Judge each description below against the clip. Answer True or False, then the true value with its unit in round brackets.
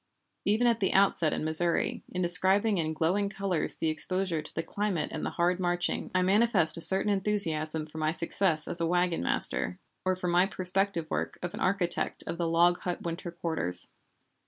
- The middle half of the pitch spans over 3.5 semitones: False (2.8 semitones)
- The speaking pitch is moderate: True (175 Hz)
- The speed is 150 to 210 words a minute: True (190 wpm)